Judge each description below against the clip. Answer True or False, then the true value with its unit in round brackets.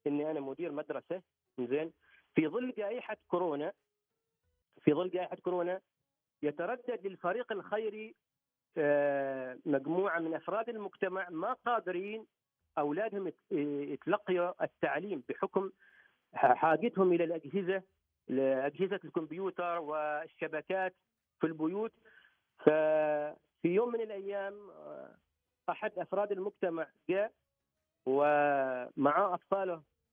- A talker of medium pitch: True (175 Hz)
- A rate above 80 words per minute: True (90 wpm)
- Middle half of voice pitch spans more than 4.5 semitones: True (5.1 semitones)